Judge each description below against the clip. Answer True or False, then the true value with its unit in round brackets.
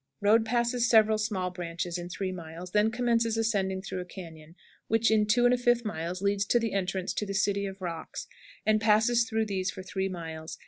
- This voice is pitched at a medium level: False (200 Hz)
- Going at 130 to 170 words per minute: False (195 wpm)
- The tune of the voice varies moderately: True (3.6 semitones)